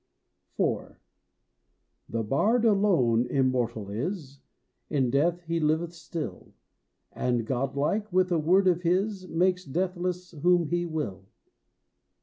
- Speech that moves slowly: Yes, slow, 115 wpm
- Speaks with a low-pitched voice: No, medium, 165 Hz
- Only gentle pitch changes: No, wide, 5.4 semitones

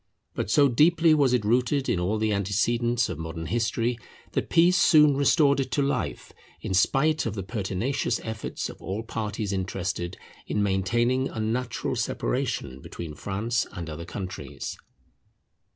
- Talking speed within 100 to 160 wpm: Yes, average, 150 wpm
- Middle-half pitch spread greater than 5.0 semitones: Yes, wide, 5.5 semitones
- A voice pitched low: Yes, low, 110 Hz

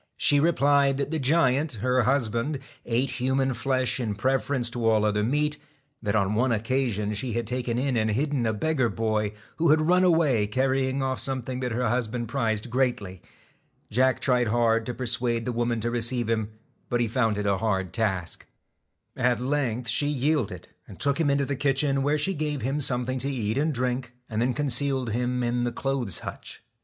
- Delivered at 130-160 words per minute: No, average, 190 wpm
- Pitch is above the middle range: No, low, 125 Hz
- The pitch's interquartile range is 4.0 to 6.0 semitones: No, average, 3.3 semitones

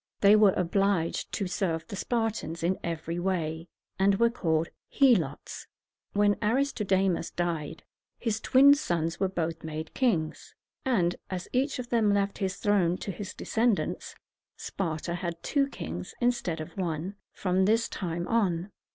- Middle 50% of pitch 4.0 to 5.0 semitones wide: Yes, average, 4.4 semitones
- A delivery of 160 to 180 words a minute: No, average, 145 wpm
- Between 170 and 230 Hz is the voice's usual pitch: Yes, high, 190 Hz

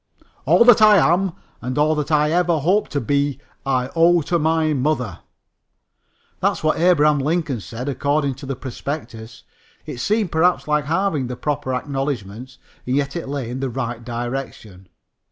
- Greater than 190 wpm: No, average, 165 wpm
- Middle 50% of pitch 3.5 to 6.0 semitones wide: Yes, average, 4.0 semitones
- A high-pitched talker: No, medium, 145 Hz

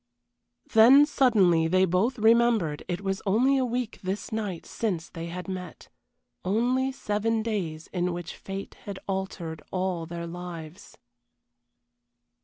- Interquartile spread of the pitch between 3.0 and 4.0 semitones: No, average, 4.4 semitones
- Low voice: No, high, 195 Hz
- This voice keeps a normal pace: No, slow, 130 wpm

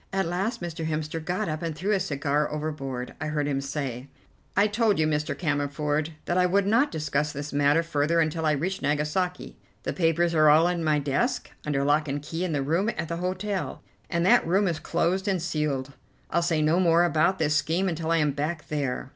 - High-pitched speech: No, medium, 160 Hz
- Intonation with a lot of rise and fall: No, average, 3.0 semitones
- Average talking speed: No, fast, 215 wpm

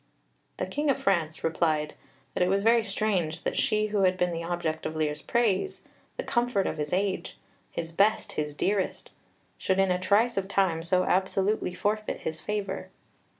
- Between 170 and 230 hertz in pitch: Yes, high, 190 Hz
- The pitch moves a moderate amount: Yes, average, 4.0 semitones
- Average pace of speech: Yes, average, 180 wpm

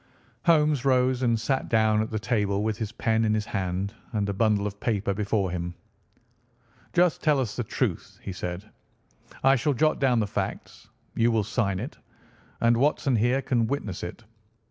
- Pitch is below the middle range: Yes, low, 110 Hz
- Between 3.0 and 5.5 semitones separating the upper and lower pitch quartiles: Yes, average, 4.0 semitones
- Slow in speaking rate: No, average, 180 wpm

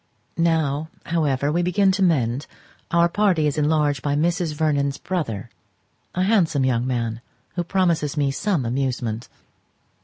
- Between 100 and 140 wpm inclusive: Yes, slow, 135 wpm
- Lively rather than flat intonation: No, average, 4.4 semitones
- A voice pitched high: No, medium, 150 Hz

